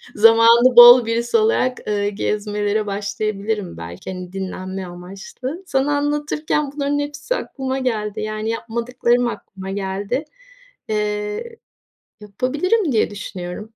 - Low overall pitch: No, high, 220 Hz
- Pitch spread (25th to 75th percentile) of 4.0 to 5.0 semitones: Yes, average, 4.6 semitones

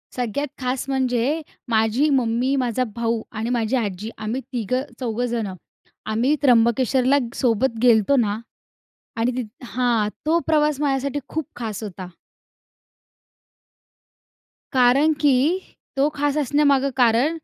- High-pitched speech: Yes, very high, 250 Hz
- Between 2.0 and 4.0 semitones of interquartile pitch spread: Yes, average, 3.4 semitones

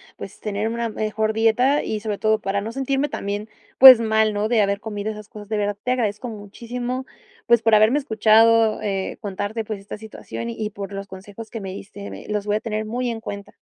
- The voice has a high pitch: Yes, high, 215 Hz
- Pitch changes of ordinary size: No, narrow, 1.9 semitones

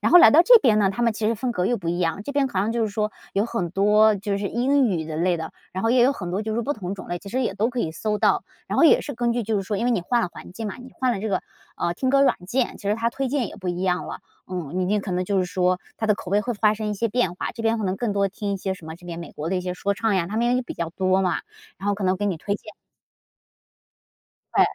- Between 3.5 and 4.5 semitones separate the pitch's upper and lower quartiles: Yes, average, 4.1 semitones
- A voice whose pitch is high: Yes, high, 205 Hz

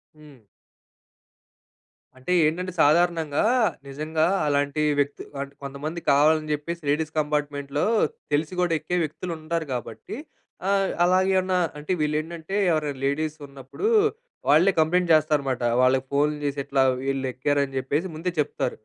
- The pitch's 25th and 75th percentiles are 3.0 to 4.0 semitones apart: No, narrow, 2.6 semitones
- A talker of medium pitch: Yes, medium, 150 Hz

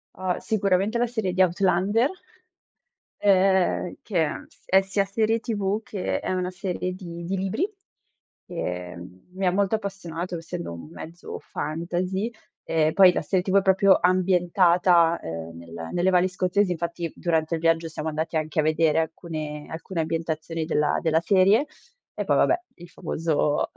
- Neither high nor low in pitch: Yes, medium, 175 Hz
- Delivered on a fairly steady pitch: No, average, 3.0 semitones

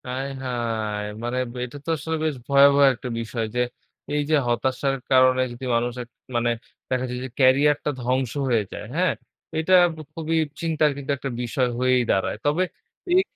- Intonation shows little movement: No, average, 3.1 semitones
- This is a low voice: Yes, low, 130 Hz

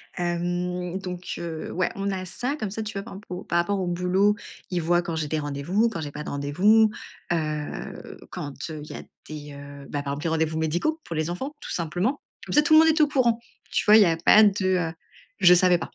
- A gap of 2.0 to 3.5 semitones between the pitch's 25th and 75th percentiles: No, average, 4.3 semitones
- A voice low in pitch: No, medium, 175 Hz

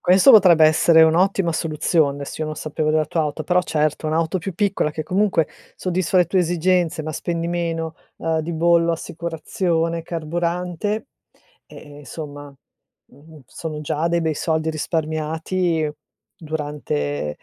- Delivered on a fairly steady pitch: Yes, narrow, 1.9 semitones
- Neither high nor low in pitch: Yes, medium, 160 Hz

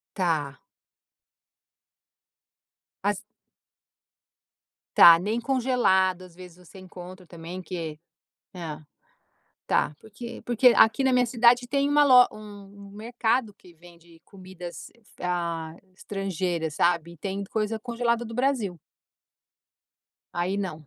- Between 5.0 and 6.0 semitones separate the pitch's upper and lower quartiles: Yes, average, 5.3 semitones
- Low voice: No, high, 190 Hz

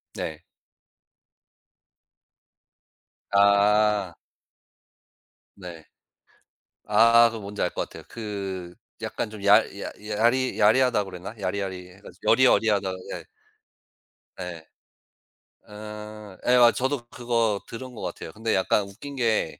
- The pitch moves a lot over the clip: No, average, 3.1 semitones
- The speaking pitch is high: No, low, 105 Hz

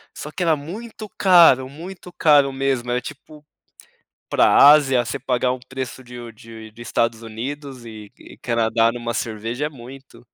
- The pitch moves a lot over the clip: No, average, 3.8 semitones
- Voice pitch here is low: Yes, low, 130 Hz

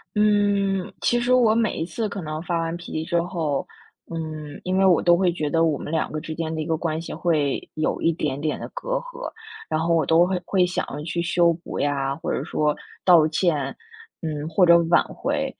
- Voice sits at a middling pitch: Yes, medium, 165 Hz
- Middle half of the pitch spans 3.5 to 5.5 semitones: No, average, 2.9 semitones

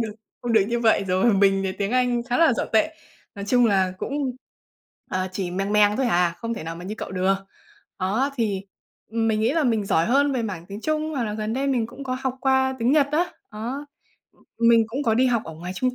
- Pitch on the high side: Yes, high, 230 Hz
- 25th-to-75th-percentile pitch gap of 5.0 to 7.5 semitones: No, average, 4.6 semitones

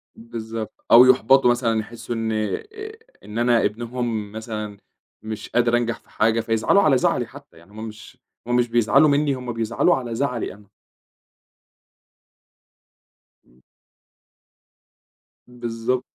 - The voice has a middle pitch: No, low, 115 Hz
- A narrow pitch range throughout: Yes, narrow, 2.0 semitones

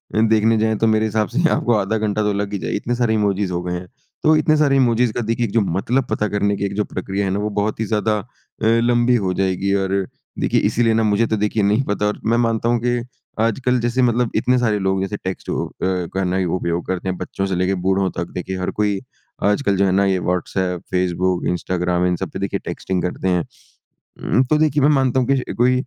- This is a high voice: No, low, 105 Hz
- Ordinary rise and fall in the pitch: Yes, average, 3.7 semitones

